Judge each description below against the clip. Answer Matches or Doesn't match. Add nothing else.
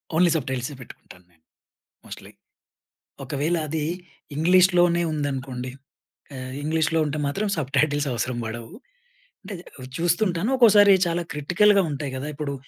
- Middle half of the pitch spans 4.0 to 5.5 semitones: Matches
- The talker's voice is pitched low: Doesn't match